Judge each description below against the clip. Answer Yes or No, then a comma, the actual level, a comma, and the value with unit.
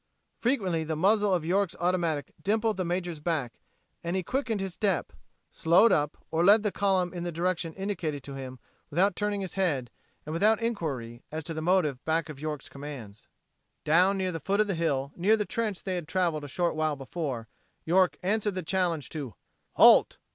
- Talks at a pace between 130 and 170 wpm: No, average, 190 wpm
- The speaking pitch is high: No, medium, 175 Hz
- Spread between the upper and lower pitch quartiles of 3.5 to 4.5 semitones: Yes, average, 4.2 semitones